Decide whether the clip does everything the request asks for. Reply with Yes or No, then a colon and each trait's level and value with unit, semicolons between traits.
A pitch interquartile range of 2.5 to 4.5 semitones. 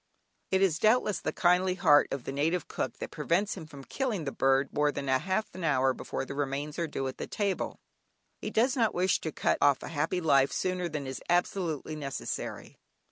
No: average, 5.0 semitones